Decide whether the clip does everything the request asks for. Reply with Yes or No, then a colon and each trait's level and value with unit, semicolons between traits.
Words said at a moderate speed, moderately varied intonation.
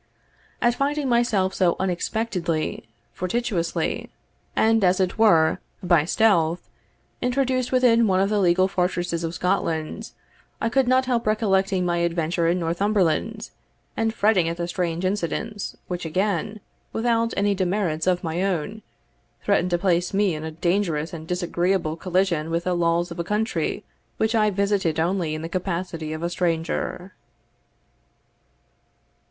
Yes: average, 145 wpm; average, 3.9 semitones